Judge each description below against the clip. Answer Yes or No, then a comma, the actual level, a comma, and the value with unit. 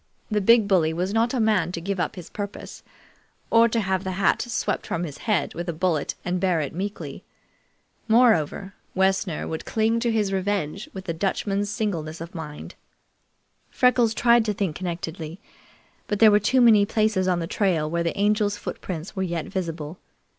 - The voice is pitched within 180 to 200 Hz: Yes, high, 190 Hz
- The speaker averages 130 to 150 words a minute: No, average, 180 wpm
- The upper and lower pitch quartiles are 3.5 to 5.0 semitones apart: Yes, average, 4.0 semitones